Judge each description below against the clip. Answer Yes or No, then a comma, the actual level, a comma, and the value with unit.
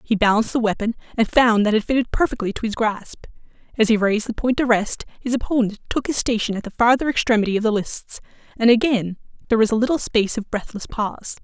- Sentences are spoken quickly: Yes, fast, 220 wpm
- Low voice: No, high, 225 Hz